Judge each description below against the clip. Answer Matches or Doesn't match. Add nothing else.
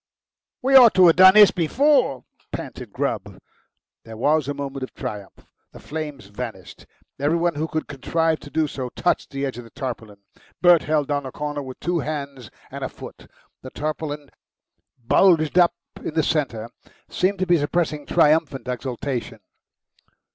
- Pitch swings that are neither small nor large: Matches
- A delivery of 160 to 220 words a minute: Matches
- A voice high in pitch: Doesn't match